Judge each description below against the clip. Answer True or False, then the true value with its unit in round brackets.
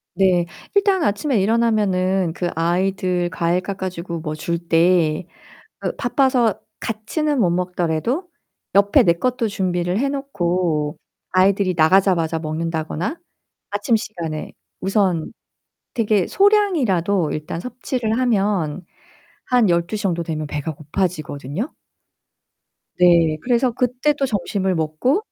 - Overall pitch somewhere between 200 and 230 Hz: False (185 Hz)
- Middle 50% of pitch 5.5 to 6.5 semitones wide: False (5.1 semitones)